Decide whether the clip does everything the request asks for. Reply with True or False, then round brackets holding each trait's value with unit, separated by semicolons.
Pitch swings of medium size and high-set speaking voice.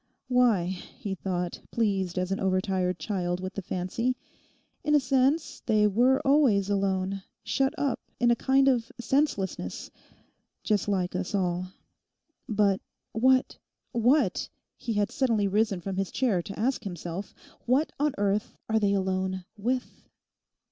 True (4.9 semitones; 205 Hz)